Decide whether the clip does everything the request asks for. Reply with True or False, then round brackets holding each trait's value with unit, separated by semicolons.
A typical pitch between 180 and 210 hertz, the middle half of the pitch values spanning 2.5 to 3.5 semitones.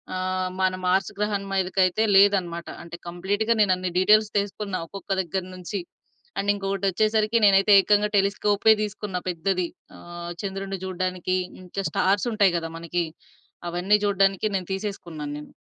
False (195 Hz; 2.0 semitones)